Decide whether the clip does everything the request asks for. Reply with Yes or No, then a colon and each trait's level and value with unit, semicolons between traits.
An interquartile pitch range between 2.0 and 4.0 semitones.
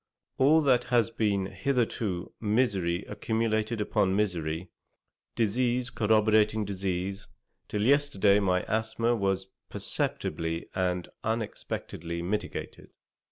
Yes: average, 3.4 semitones